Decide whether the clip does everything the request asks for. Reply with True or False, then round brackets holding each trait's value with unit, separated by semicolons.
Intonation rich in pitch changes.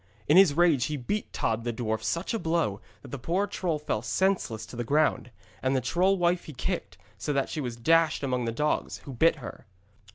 True (6.1 semitones)